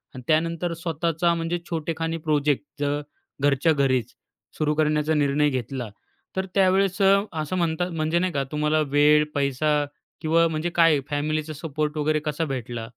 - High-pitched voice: No, medium, 155 Hz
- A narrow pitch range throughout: Yes, narrow, 2.3 semitones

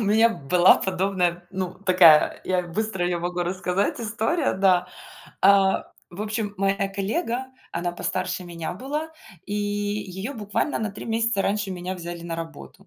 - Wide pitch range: No, average, 2.9 semitones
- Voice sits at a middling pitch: No, high, 195 Hz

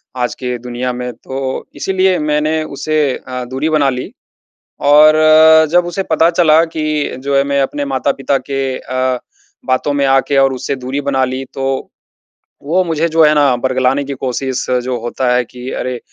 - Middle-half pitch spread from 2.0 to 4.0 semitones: Yes, average, 3.0 semitones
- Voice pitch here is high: No, low, 135 Hz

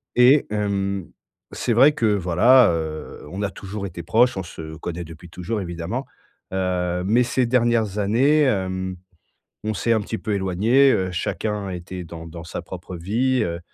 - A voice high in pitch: No, low, 100 Hz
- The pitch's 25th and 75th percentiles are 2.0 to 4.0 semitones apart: No, average, 4.6 semitones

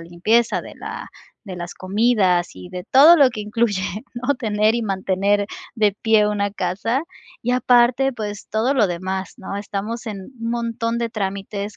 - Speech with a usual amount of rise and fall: Yes, average, 3.4 semitones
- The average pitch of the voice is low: No, high, 210 Hz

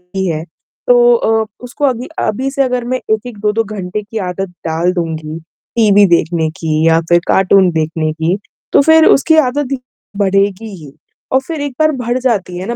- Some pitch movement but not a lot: No, wide, 6.3 semitones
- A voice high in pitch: Yes, high, 205 Hz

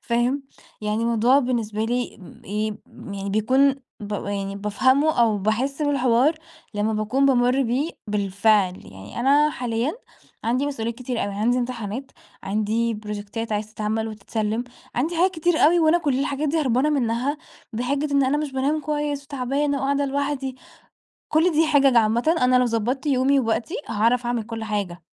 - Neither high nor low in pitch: No, high, 245 Hz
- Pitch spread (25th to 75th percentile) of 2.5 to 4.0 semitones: No, average, 4.4 semitones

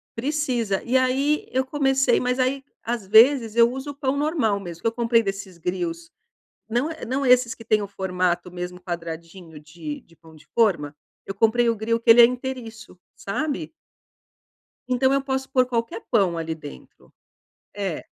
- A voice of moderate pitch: No, high, 230 Hz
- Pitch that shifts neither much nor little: No, wide, 6.3 semitones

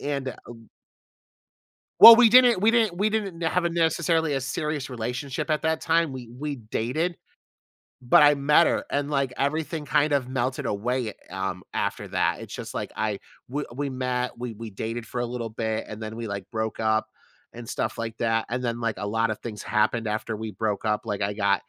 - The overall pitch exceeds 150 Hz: No, low, 125 Hz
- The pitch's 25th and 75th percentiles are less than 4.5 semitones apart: No, average, 5.2 semitones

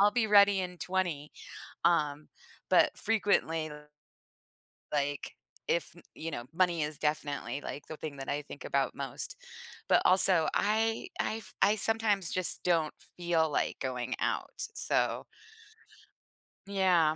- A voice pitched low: No, medium, 170 Hz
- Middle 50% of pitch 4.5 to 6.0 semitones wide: Yes, average, 5.0 semitones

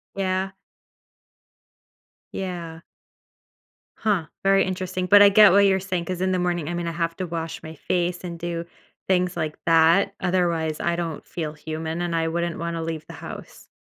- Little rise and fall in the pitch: Yes, narrow, 2.1 semitones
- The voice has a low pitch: No, medium, 175 Hz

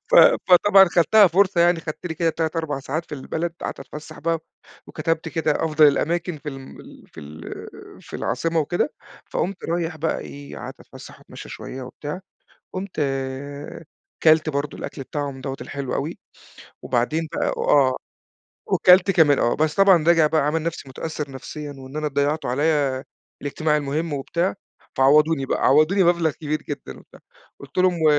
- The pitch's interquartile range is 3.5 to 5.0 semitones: No, average, 2.9 semitones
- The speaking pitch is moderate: Yes, medium, 155 Hz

